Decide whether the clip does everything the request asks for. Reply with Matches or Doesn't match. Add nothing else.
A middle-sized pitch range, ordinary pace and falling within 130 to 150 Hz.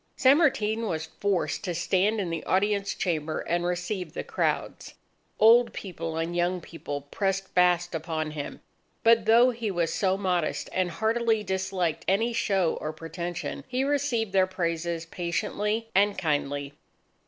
Doesn't match